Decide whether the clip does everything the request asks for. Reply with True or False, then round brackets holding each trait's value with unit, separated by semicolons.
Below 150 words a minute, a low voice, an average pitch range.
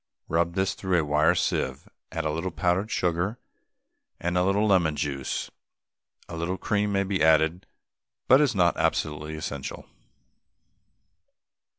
True (135 wpm; 85 Hz; 3.4 semitones)